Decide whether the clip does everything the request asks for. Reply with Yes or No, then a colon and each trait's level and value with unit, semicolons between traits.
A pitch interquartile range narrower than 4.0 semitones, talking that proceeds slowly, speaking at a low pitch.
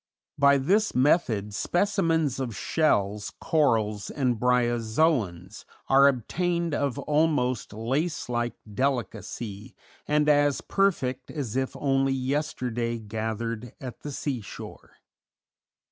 No: average, 4.4 semitones; slow, 105 wpm; low, 130 Hz